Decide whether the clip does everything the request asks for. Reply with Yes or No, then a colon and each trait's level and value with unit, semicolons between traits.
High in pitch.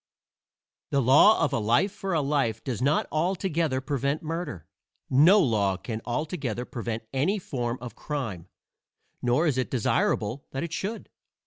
No: low, 135 Hz